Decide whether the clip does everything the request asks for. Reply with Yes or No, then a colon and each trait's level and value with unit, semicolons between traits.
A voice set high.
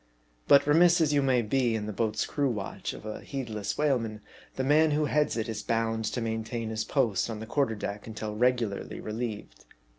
No: low, 115 Hz